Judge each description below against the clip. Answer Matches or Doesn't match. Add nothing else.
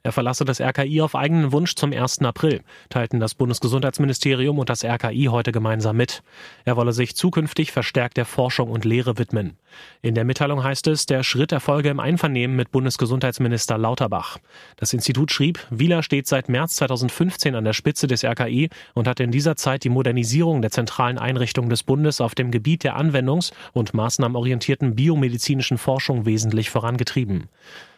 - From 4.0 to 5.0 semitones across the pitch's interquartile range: Doesn't match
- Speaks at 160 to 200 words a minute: Matches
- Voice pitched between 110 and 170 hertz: Matches